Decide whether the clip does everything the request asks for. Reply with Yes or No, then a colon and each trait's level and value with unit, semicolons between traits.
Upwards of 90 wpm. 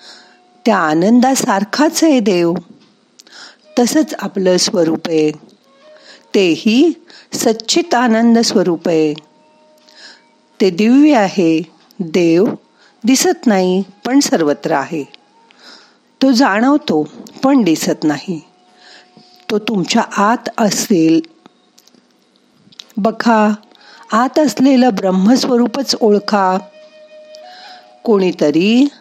No: slow, 80 wpm